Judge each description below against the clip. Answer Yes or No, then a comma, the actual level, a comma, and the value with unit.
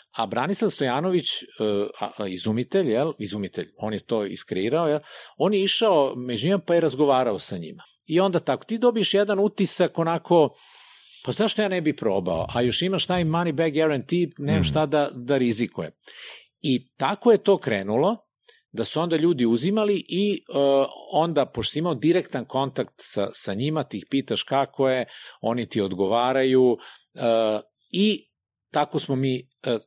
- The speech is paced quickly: Yes, fast, 165 wpm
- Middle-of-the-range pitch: Yes, medium, 150 Hz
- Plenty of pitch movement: Yes, wide, 6.6 semitones